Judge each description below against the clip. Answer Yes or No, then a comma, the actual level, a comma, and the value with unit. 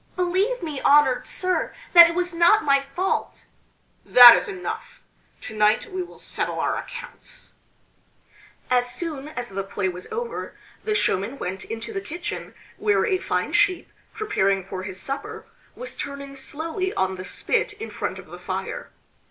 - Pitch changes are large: Yes, wide, 8.7 semitones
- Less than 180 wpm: Yes, average, 160 wpm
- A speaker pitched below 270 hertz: No, very high, 300 Hz